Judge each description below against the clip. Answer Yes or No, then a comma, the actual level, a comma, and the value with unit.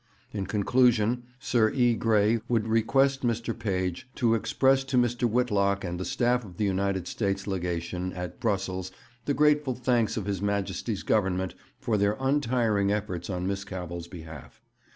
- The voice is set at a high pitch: No, low, 105 Hz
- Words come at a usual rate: Yes, average, 155 wpm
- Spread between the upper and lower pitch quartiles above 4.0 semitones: Yes, average, 4.4 semitones